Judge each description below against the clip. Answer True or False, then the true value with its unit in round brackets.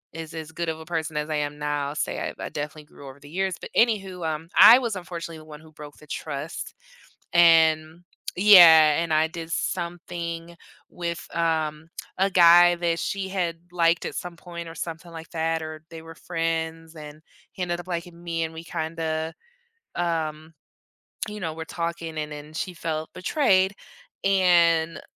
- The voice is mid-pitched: True (165 Hz)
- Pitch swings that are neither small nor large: False (1.6 semitones)